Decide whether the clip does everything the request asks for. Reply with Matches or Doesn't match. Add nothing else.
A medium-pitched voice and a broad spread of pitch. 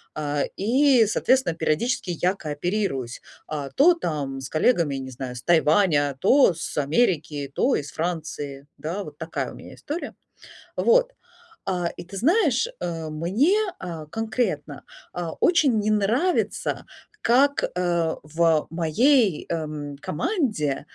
Matches